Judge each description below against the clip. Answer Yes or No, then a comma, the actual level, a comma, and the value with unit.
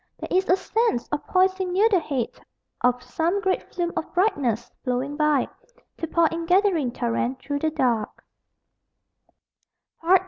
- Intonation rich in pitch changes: Yes, wide, 6.7 semitones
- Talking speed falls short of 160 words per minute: Yes, average, 145 wpm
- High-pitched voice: Yes, very high, 315 Hz